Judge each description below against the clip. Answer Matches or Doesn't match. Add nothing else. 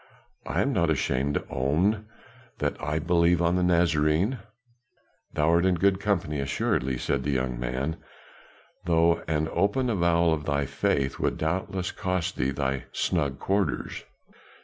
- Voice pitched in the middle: Doesn't match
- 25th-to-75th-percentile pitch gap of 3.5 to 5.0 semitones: Matches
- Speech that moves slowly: Doesn't match